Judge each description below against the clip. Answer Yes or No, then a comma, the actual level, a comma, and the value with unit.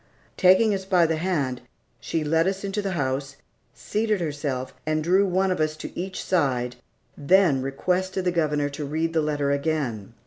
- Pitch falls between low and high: Yes, medium, 160 Hz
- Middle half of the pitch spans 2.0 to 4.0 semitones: No, average, 4.7 semitones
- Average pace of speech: Yes, average, 175 wpm